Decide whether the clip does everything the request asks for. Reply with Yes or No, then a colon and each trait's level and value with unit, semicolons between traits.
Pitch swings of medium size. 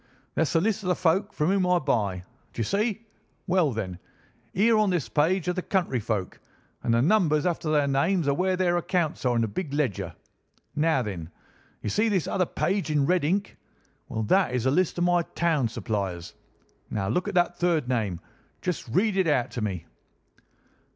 No: wide, 7.3 semitones